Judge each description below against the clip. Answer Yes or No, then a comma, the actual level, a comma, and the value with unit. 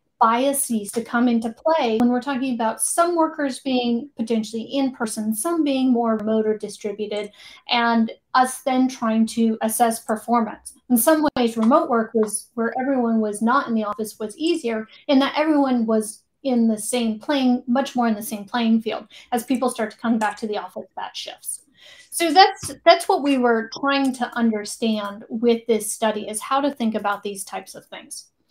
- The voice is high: Yes, high, 235 Hz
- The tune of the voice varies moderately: Yes, average, 3.4 semitones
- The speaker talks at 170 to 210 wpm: Yes, average, 190 wpm